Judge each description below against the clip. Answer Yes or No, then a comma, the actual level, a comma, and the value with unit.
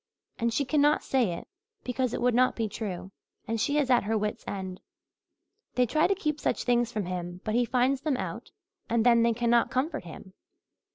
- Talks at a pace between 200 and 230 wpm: Yes, fast, 205 wpm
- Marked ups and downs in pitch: No, average, 3.6 semitones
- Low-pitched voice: No, high, 235 Hz